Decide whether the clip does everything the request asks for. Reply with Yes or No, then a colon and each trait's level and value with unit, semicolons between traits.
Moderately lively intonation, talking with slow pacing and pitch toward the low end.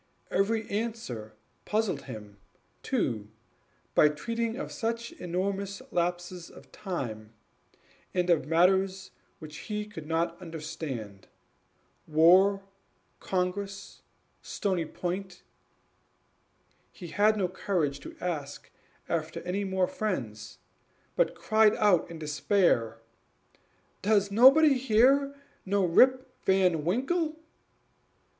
No: average, 4.8 semitones; slow, 100 wpm; medium, 185 Hz